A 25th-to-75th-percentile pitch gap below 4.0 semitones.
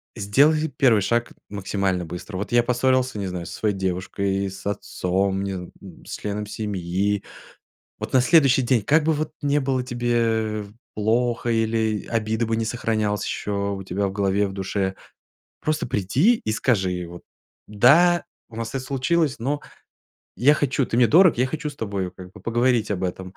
No: average, 4.6 semitones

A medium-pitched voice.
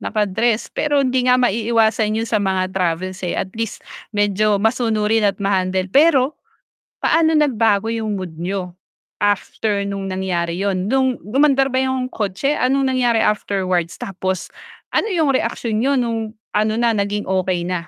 No: high, 215 Hz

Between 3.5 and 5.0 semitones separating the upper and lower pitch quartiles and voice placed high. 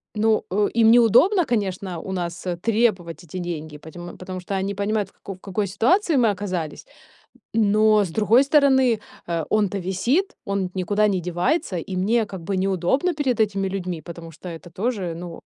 Yes: average, 3.8 semitones; high, 195 Hz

